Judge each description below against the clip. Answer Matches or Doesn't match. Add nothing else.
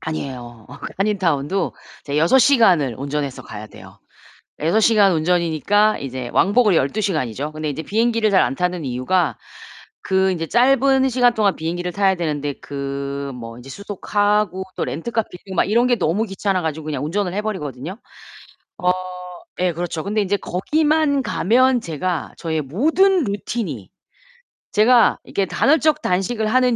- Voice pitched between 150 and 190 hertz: Matches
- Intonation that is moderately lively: Doesn't match